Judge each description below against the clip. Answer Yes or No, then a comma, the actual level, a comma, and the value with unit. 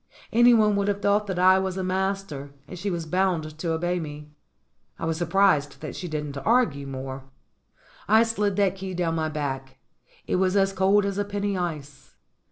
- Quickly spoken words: No, average, 185 wpm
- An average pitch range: Yes, average, 4.4 semitones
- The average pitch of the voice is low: No, medium, 185 Hz